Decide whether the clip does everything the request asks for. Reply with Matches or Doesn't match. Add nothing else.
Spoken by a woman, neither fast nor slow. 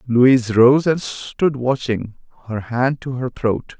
Doesn't match